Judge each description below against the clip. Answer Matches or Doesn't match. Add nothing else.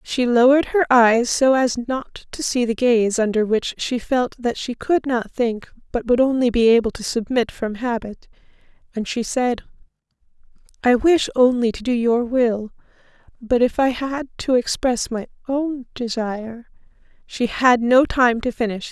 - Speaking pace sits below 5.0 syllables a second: Matches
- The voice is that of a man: Doesn't match